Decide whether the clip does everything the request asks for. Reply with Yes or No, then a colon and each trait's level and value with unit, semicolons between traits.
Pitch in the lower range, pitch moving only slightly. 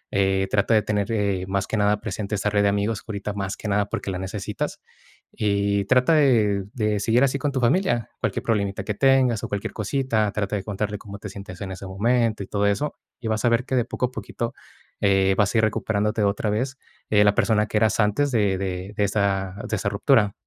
Yes: low, 105 Hz; narrow, 2.3 semitones